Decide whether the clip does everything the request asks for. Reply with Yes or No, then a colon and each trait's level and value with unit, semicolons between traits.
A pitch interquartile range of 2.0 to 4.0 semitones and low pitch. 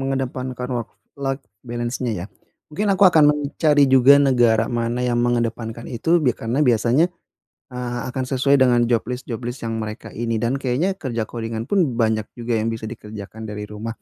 Yes: average, 2.8 semitones; low, 120 Hz